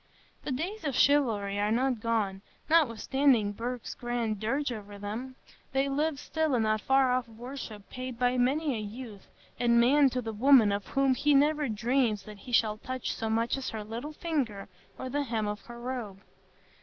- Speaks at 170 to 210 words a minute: Yes, average, 185 wpm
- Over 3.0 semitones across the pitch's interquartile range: Yes, average, 3.9 semitones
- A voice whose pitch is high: Yes, high, 245 Hz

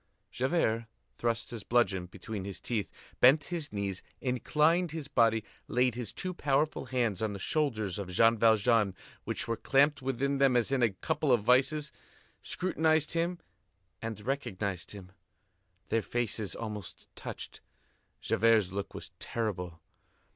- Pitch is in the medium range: No, low, 115 Hz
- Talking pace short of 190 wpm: Yes, average, 140 wpm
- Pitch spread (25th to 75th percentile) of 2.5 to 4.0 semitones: No, average, 5.1 semitones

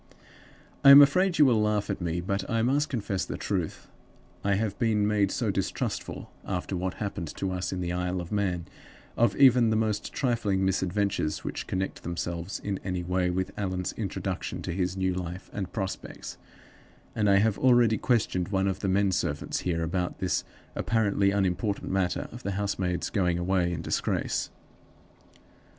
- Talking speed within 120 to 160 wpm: No, average, 170 wpm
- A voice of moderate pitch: No, very low, 95 Hz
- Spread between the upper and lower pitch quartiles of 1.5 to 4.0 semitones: Yes, average, 2.8 semitones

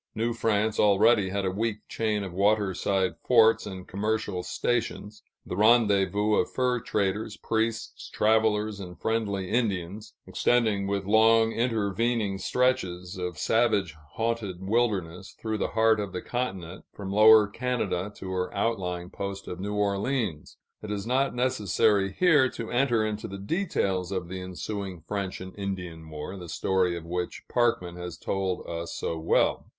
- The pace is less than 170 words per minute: Yes, average, 150 wpm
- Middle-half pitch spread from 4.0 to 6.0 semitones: No, average, 3.2 semitones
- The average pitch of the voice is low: Yes, low, 100 Hz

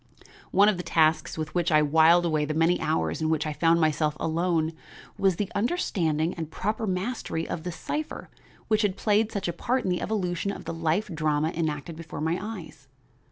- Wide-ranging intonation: No, average, 3.8 semitones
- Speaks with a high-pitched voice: No, medium, 165 Hz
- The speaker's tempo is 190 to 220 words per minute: Yes, average, 200 wpm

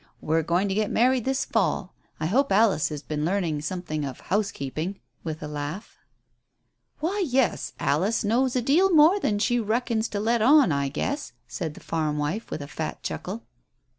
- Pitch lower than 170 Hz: No, high, 200 Hz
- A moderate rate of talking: Yes, average, 180 wpm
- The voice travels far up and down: Yes, wide, 7.7 semitones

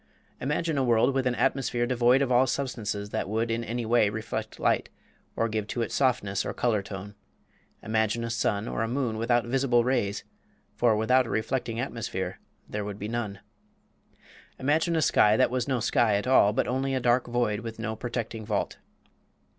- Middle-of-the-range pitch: No, low, 115 Hz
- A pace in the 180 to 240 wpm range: Yes, average, 185 wpm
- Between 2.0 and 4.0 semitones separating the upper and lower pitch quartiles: Yes, average, 2.7 semitones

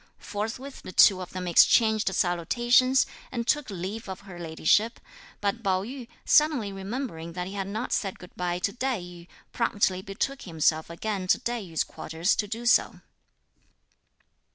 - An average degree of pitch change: Yes, average, 4.7 semitones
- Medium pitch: No, high, 200 Hz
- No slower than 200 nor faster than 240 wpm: No, average, 160 wpm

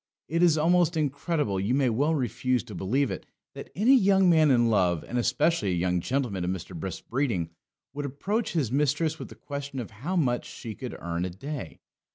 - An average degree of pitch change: No, wide, 7.5 semitones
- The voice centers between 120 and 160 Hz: Yes, low, 135 Hz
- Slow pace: No, average, 200 wpm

